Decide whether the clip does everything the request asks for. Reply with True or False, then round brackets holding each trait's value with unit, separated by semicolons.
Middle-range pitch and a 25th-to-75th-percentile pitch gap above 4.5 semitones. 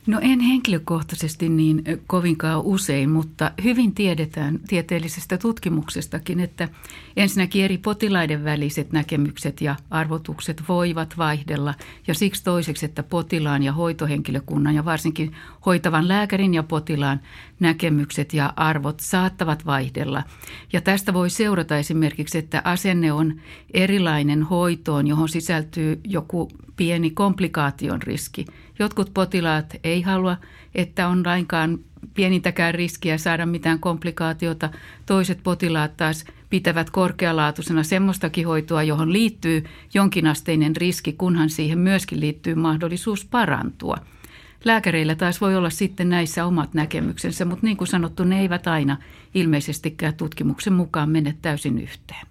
False (165 Hz; 2.8 semitones)